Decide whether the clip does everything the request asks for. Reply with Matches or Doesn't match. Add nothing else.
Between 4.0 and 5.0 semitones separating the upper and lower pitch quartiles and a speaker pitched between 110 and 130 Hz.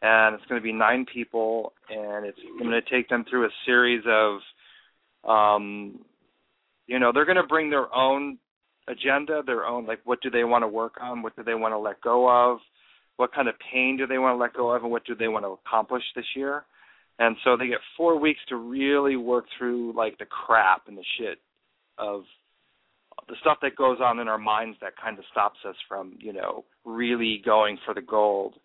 Doesn't match